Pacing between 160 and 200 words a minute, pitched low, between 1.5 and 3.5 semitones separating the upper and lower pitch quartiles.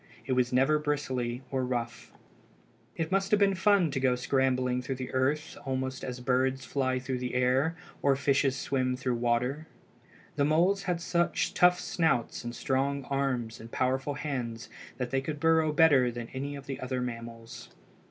Yes: average, 165 wpm; low, 130 Hz; average, 2.9 semitones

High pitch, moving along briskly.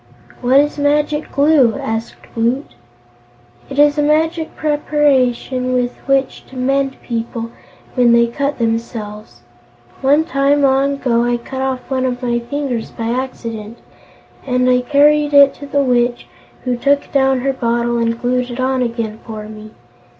No: very high, 255 Hz; average, 155 wpm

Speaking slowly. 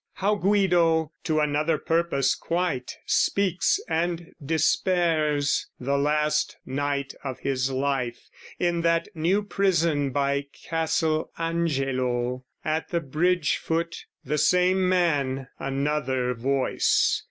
Yes: slow, 110 wpm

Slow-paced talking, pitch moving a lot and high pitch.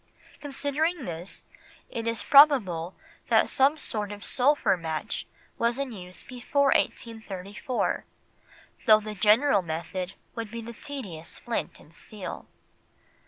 Yes: slow, 120 wpm; wide, 6.4 semitones; high, 225 Hz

